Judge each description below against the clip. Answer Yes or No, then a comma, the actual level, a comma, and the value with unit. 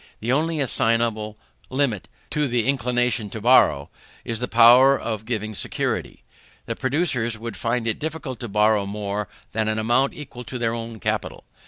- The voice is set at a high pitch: No, low, 115 Hz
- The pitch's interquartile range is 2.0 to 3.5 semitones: Yes, average, 3.0 semitones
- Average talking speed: Yes, average, 165 wpm